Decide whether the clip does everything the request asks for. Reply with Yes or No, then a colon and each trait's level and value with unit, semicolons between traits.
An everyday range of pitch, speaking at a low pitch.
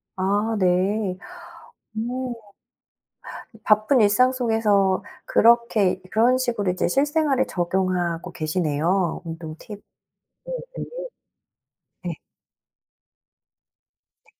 No: average, 4.6 semitones; high, 205 Hz